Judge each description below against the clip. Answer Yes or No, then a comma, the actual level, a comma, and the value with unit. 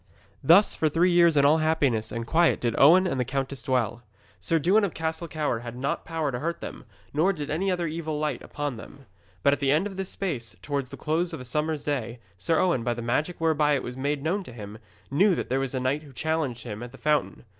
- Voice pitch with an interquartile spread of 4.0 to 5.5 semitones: Yes, average, 4.4 semitones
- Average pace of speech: No, fast, 245 wpm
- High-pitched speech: No, medium, 150 Hz